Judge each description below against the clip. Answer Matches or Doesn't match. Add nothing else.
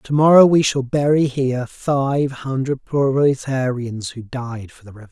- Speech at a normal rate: Matches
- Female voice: Doesn't match